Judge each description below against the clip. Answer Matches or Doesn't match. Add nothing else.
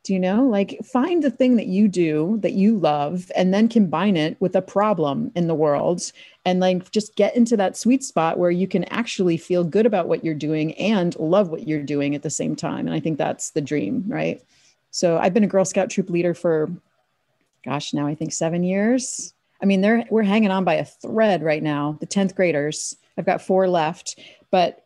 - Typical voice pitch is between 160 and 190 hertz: Matches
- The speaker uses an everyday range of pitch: Matches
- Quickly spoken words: Matches